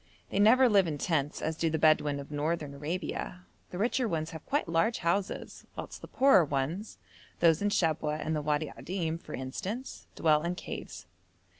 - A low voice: No, medium, 165 Hz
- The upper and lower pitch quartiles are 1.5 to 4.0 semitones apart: No, average, 4.4 semitones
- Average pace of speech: Yes, average, 180 wpm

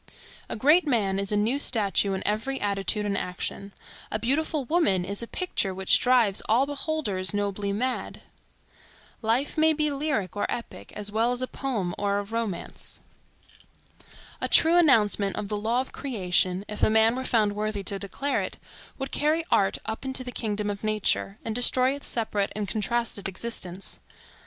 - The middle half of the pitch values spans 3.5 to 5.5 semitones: Yes, average, 4.4 semitones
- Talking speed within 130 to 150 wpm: No, average, 175 wpm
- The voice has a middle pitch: No, high, 215 Hz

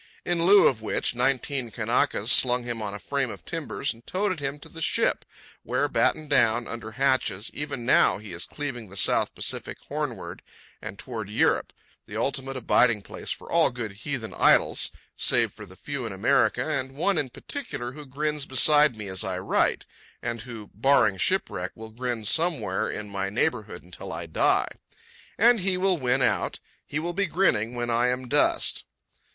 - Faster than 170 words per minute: Yes, average, 180 wpm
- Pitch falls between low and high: No, low, 125 Hz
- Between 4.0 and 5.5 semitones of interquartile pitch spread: Yes, average, 5.1 semitones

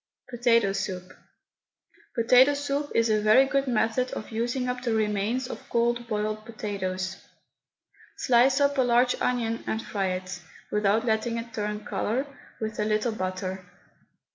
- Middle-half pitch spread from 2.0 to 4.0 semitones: Yes, average, 3.0 semitones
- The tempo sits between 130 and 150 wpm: Yes, average, 145 wpm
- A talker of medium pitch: No, high, 225 Hz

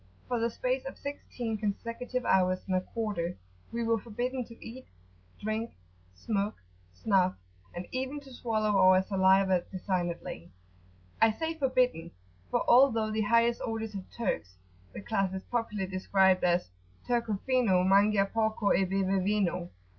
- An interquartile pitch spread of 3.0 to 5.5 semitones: Yes, average, 3.7 semitones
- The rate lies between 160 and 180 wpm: No, average, 145 wpm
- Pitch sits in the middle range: No, high, 210 Hz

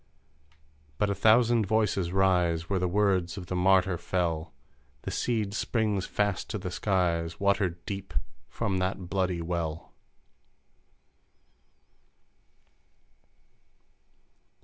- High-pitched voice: No, very low, 95 Hz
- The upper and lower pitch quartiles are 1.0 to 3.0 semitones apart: Yes, narrow, 2.5 semitones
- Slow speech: Yes, slow, 100 wpm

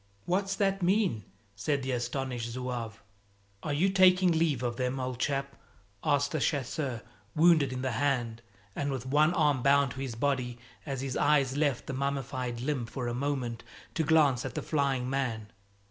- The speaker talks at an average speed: Yes, average, 175 wpm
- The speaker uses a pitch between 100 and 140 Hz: Yes, low, 135 Hz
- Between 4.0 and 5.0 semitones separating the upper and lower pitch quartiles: No, average, 3.0 semitones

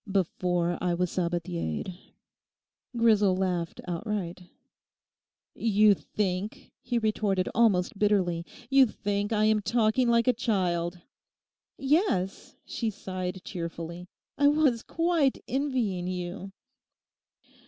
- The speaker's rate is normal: No, slow, 100 wpm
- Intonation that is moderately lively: Yes, average, 4.3 semitones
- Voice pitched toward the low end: No, high, 200 Hz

